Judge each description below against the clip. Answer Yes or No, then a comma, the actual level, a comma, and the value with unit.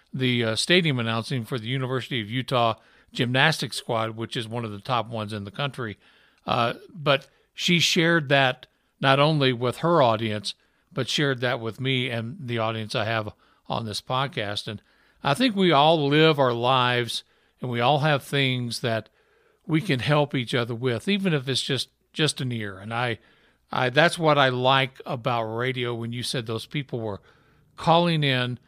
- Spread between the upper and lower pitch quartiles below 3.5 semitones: No, average, 3.8 semitones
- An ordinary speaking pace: Yes, average, 185 wpm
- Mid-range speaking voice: No, low, 130 Hz